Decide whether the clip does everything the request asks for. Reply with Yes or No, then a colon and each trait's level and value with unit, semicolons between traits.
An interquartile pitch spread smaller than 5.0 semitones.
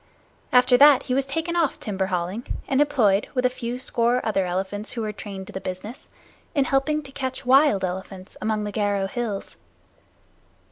No: average, 5.3 semitones